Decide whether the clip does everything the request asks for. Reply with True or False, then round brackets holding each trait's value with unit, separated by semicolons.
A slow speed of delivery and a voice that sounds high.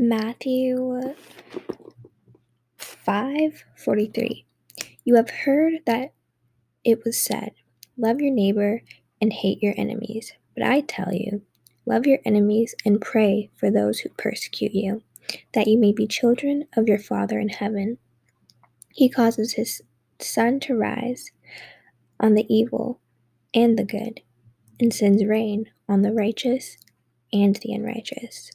True (130 wpm; 220 Hz)